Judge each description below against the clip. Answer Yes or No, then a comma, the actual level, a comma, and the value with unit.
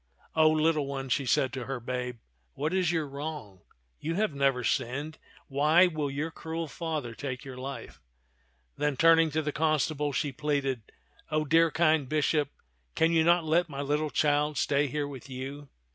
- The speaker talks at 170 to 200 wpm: Yes, average, 185 wpm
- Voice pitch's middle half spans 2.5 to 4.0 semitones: Yes, average, 2.8 semitones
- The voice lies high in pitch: No, medium, 145 Hz